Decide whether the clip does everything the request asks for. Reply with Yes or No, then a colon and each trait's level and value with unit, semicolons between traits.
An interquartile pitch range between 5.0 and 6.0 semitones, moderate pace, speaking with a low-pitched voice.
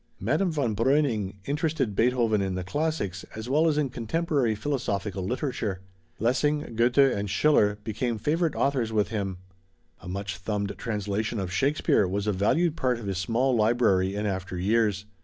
Yes: average, 5.3 semitones; average, 160 wpm; low, 110 Hz